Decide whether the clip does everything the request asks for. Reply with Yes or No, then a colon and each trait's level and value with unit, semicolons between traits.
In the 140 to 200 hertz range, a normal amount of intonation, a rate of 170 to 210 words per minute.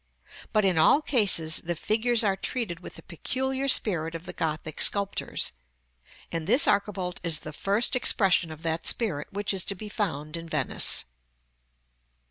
No: high, 190 Hz; average, 4.8 semitones; average, 160 wpm